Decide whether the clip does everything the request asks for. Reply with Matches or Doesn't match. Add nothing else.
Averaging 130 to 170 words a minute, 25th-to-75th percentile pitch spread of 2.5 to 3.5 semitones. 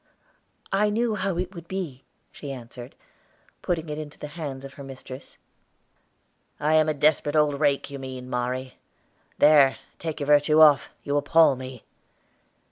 Matches